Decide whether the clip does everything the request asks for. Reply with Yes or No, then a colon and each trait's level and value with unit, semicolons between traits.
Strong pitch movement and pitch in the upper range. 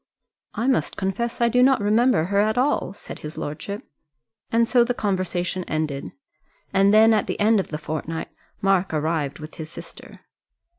Yes: wide, 6.1 semitones; high, 195 Hz